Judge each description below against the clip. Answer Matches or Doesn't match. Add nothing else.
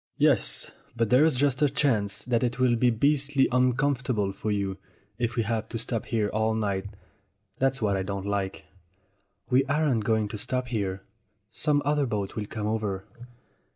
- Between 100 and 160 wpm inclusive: Doesn't match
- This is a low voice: Matches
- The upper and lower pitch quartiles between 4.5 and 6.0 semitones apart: Doesn't match